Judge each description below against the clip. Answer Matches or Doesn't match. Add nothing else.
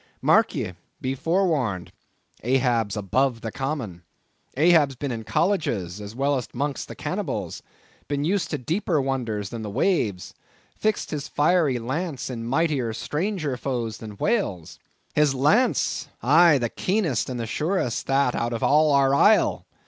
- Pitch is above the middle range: Doesn't match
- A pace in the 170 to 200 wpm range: Doesn't match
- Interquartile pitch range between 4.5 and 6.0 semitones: Matches